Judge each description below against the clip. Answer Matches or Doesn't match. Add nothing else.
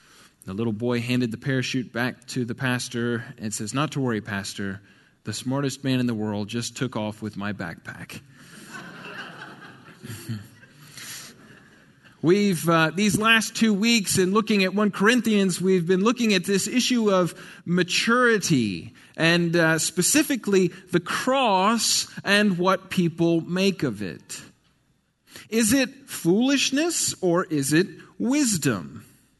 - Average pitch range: Doesn't match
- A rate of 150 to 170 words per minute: Doesn't match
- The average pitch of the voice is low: Doesn't match